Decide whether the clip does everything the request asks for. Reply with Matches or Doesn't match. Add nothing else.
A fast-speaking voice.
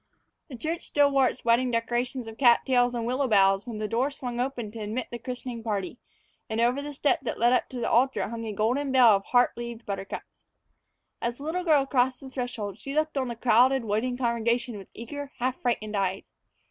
Matches